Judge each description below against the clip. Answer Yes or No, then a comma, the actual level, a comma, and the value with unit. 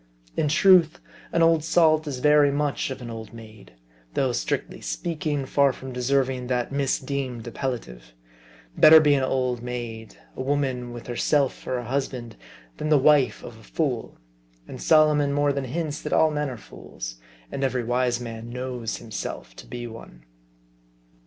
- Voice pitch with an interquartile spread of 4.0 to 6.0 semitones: No, average, 3.4 semitones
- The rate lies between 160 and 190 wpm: Yes, average, 165 wpm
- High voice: No, low, 130 Hz